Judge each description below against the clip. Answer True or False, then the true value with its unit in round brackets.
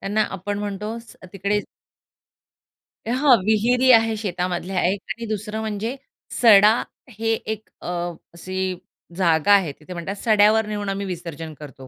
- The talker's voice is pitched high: True (205 Hz)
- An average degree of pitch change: True (3.0 semitones)